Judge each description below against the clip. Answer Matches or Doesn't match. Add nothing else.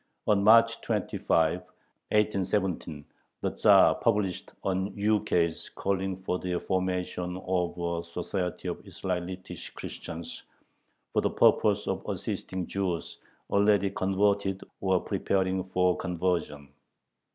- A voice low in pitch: Matches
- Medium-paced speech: Doesn't match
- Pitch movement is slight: Matches